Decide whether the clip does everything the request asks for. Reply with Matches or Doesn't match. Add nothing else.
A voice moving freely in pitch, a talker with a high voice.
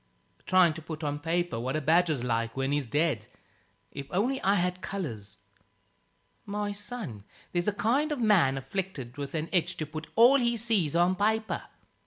Doesn't match